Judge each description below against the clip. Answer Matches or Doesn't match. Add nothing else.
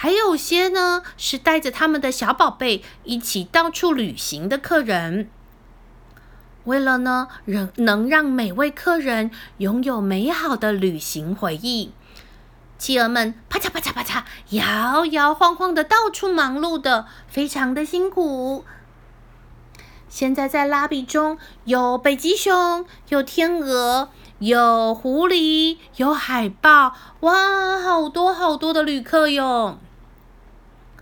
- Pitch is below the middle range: Doesn't match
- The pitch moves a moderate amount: Doesn't match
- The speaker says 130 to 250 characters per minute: Matches